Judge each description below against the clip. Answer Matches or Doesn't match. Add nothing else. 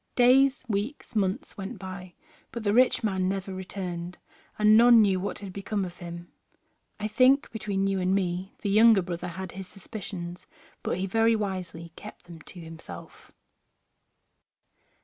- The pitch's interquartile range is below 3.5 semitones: Matches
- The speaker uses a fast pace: Doesn't match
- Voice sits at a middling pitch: Doesn't match